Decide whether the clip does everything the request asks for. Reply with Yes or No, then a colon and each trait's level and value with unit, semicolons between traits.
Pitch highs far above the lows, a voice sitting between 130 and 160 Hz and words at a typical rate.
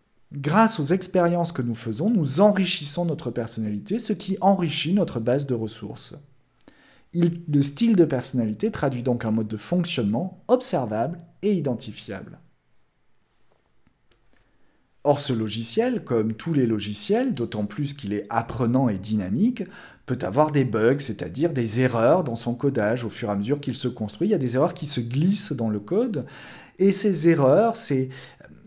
Yes: wide, 7.5 semitones; medium, 140 Hz; average, 165 wpm